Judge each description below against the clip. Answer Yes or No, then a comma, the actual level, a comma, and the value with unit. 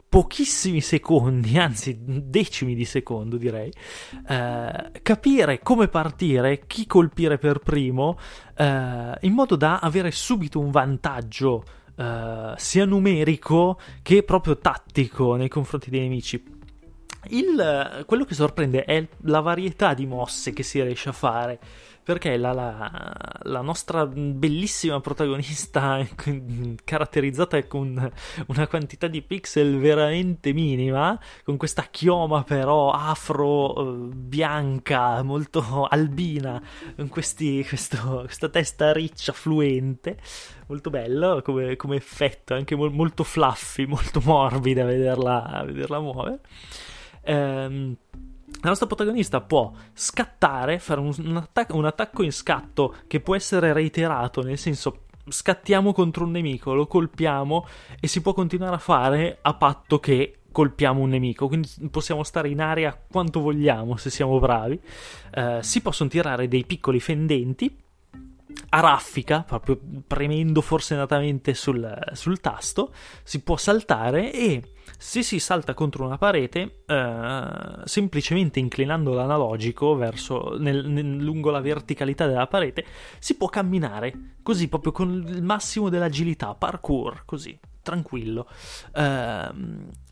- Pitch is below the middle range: No, medium, 145 Hz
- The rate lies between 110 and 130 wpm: Yes, average, 125 wpm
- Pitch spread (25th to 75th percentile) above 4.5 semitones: No, average, 4.2 semitones